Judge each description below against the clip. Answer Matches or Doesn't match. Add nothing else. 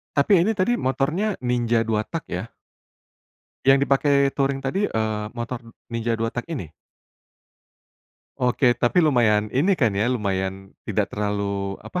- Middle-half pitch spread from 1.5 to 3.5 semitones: Doesn't match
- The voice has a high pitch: Doesn't match